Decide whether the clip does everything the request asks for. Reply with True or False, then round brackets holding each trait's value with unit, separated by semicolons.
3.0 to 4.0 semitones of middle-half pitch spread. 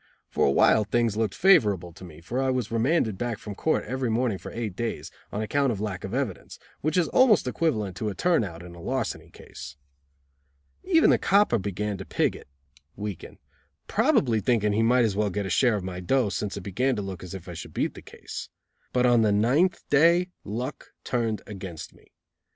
False (4.7 semitones)